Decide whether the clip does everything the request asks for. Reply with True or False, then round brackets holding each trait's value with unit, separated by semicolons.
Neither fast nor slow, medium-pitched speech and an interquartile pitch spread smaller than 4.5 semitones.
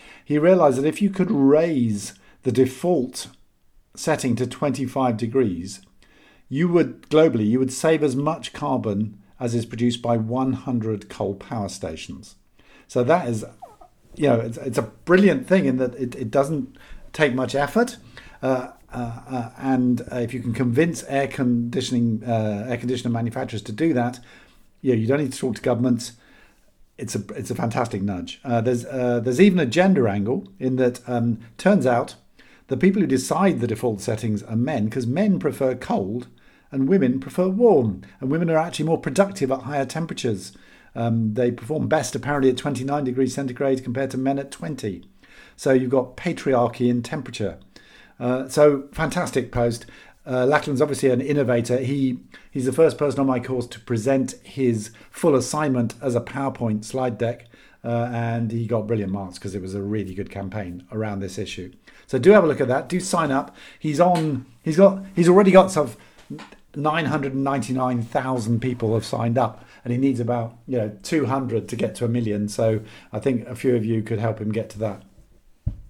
False (185 wpm; 125 Hz; 3.5 semitones)